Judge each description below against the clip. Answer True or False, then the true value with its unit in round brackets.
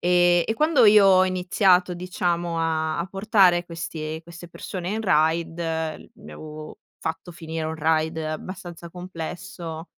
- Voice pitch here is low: False (175 Hz)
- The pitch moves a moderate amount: False (2.3 semitones)